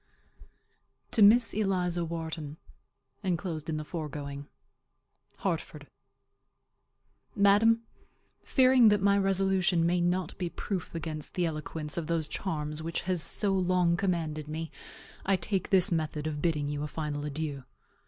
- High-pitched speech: No, medium, 170 Hz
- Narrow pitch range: No, average, 3.9 semitones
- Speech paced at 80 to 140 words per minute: Yes, slow, 135 wpm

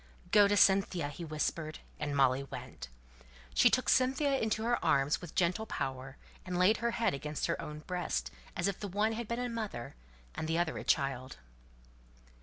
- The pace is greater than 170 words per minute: Yes, average, 185 wpm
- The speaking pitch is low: No, medium, 175 Hz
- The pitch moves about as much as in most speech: No, wide, 7.1 semitones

